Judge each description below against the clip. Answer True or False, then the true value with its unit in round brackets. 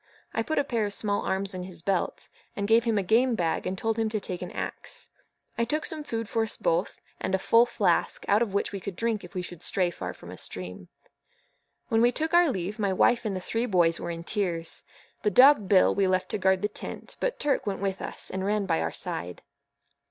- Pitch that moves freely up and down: False (3.9 semitones)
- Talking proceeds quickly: True (240 wpm)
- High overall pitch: True (200 Hz)